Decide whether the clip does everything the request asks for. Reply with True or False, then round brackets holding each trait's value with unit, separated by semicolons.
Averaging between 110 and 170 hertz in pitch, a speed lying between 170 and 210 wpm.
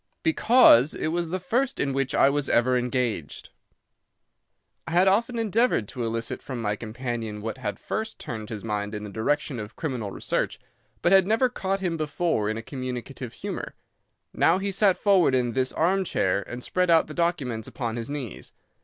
True (135 Hz; 180 wpm)